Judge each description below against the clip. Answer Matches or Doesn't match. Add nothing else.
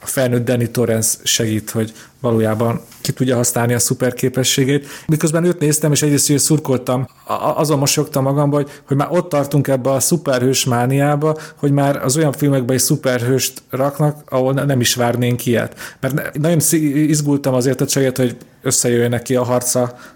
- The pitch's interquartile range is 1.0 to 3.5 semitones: Matches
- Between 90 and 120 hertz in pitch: Doesn't match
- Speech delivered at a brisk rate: Matches